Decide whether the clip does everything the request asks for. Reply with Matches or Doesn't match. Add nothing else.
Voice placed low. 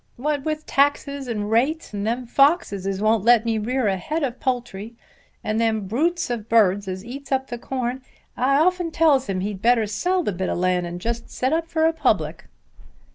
Doesn't match